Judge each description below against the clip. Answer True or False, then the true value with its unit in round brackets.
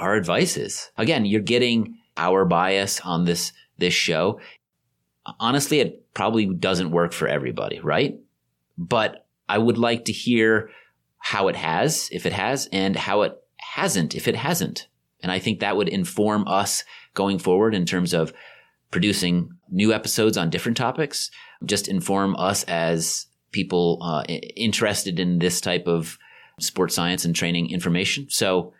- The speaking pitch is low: True (95 Hz)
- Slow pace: False (155 wpm)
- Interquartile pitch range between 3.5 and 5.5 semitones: True (4.3 semitones)